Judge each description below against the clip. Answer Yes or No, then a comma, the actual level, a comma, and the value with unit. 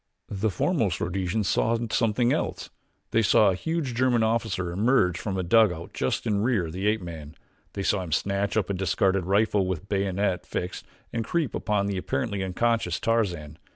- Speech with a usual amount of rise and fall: Yes, average, 3.6 semitones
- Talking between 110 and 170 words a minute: No, average, 180 wpm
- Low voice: Yes, low, 100 Hz